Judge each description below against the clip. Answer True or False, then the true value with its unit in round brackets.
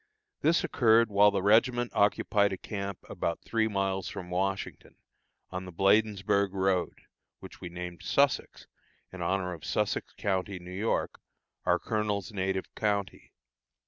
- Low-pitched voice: True (100 Hz)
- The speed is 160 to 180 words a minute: False (140 wpm)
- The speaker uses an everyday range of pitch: False (2.3 semitones)